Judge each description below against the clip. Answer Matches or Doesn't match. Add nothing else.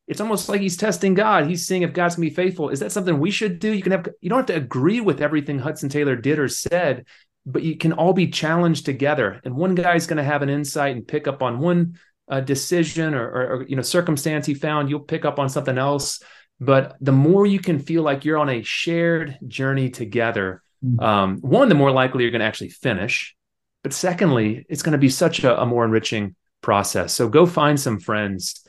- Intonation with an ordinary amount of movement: Matches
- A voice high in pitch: Doesn't match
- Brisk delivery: Matches